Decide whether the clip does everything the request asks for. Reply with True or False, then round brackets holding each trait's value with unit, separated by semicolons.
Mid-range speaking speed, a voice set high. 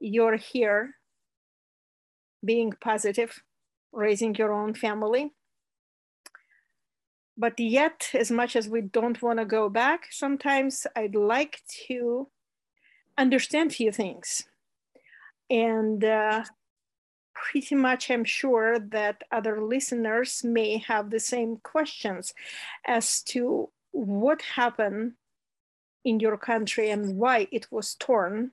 False (110 wpm; 230 Hz)